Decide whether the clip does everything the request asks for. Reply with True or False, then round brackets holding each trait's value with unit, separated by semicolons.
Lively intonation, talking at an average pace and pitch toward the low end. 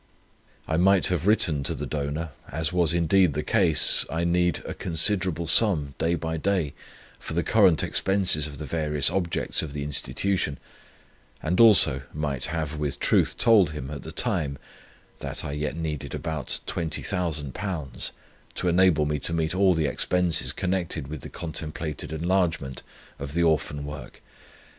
False (3.2 semitones; 160 wpm; 80 Hz)